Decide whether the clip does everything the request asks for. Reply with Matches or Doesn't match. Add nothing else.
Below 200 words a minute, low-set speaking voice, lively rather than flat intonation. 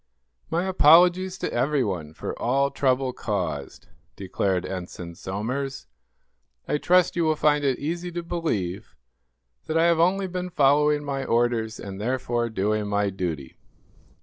Matches